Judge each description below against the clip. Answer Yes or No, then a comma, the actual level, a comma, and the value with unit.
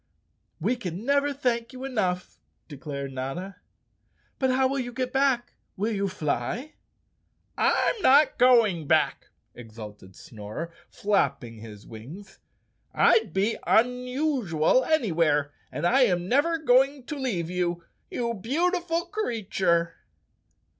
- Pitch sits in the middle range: No, high, 220 Hz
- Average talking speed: No, slow, 120 wpm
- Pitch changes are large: Yes, wide, 7.8 semitones